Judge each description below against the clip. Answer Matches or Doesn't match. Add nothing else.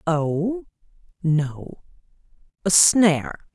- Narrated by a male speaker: Doesn't match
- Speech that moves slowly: Matches